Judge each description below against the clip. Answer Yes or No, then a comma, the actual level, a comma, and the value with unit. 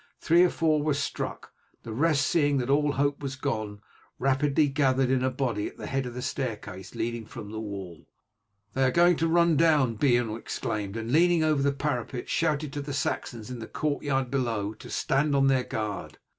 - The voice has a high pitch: No, low, 135 Hz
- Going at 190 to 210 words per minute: Yes, average, 200 wpm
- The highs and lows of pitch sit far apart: No, average, 4.0 semitones